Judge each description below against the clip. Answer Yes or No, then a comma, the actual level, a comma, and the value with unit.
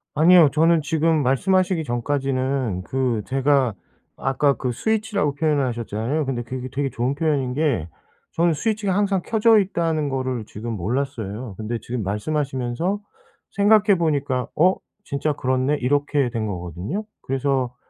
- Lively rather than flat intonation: No, average, 4.7 semitones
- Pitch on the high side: No, medium, 140 Hz